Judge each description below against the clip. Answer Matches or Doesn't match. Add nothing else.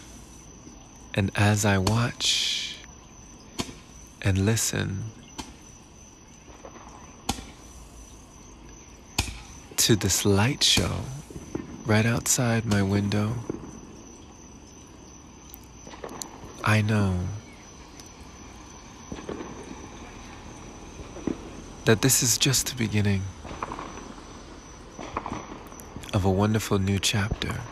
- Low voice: Matches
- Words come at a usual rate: Doesn't match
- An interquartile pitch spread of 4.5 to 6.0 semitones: Doesn't match